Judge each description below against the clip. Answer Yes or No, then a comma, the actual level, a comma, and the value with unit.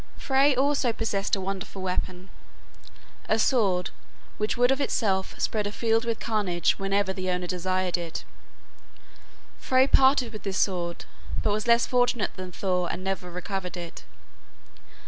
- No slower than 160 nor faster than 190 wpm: No, average, 145 wpm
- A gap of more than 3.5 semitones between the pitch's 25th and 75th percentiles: Yes, average, 4.1 semitones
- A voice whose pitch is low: No, high, 195 Hz